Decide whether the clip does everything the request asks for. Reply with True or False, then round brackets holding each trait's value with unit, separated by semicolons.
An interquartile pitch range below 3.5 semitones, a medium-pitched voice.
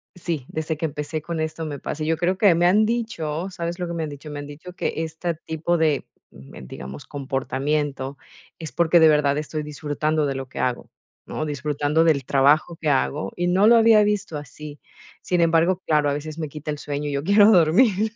True (2.9 semitones; 155 Hz)